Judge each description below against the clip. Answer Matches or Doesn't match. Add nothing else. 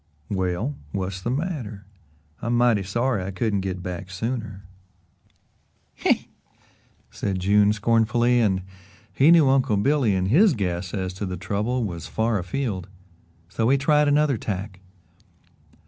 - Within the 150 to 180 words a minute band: Doesn't match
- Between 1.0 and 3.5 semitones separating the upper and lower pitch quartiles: Doesn't match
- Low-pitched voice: Matches